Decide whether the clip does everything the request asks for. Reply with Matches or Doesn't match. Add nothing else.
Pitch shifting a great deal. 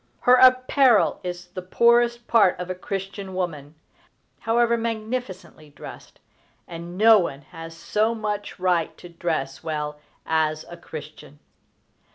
Matches